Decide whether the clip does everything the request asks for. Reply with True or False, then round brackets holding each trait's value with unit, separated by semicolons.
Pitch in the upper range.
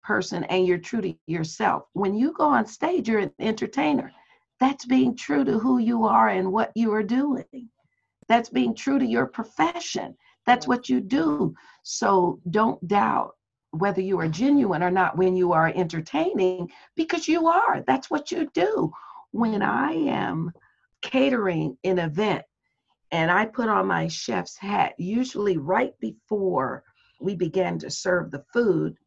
True (210 Hz)